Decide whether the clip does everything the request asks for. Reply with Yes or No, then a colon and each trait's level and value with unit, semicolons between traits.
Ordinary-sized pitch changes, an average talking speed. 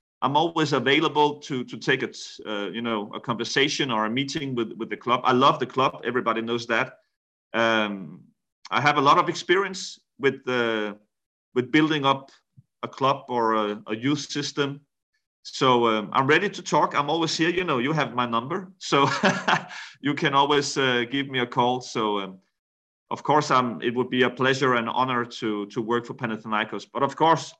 No: average, 4.2 semitones; fast, 195 wpm